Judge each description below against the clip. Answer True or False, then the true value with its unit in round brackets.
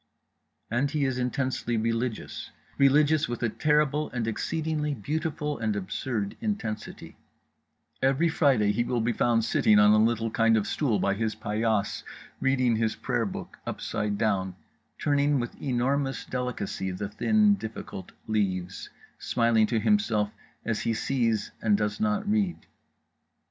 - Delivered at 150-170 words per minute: False (140 wpm)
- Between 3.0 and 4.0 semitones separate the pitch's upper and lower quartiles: False (4.9 semitones)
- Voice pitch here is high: False (120 Hz)